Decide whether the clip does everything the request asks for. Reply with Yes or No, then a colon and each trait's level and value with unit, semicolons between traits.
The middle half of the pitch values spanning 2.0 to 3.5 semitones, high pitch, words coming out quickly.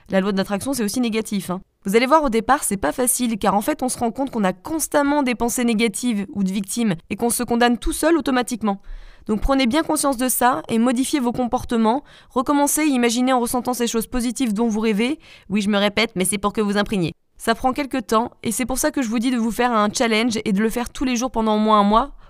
Yes: average, 3.1 semitones; high, 235 Hz; fast, 265 wpm